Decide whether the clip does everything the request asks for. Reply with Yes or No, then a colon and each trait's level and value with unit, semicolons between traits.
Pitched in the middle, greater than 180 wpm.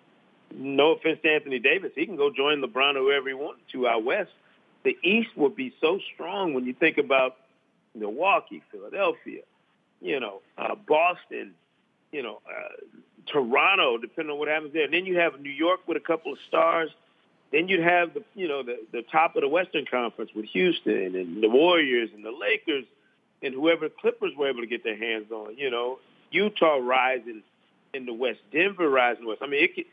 Yes: medium, 160 Hz; average, 200 wpm